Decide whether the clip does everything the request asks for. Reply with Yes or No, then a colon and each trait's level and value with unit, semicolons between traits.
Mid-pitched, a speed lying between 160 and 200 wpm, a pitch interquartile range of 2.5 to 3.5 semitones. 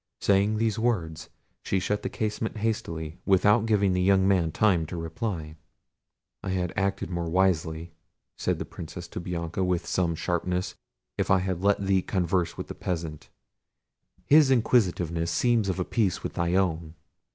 No: very low, 90 Hz; average, 165 wpm; average, 3.2 semitones